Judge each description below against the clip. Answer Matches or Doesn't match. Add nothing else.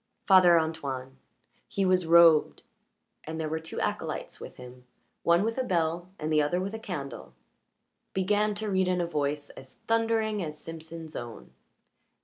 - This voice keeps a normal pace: Matches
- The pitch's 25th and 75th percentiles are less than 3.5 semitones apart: Doesn't match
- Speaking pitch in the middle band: Matches